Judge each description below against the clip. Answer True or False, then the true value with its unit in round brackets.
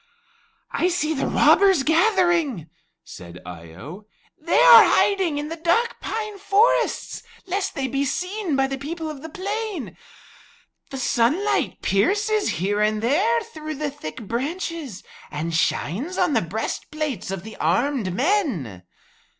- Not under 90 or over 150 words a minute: True (140 wpm)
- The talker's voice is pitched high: True (295 Hz)